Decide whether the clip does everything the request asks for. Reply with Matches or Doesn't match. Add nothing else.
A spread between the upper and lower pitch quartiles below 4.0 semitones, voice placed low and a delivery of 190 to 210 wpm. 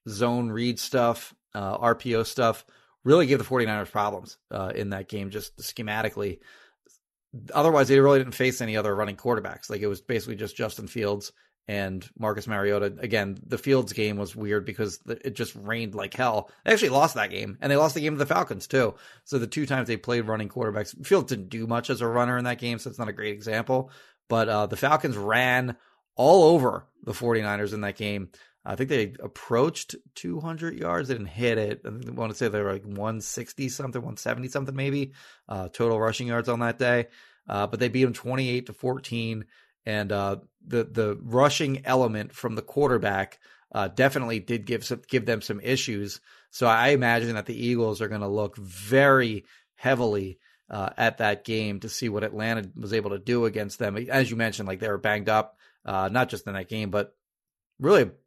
Matches